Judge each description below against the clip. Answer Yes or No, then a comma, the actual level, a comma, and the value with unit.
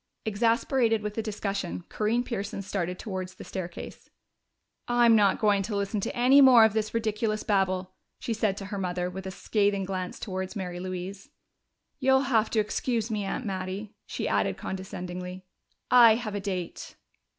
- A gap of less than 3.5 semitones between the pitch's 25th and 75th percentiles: Yes, average, 3.1 semitones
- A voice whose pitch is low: No, high, 205 Hz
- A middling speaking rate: Yes, average, 165 wpm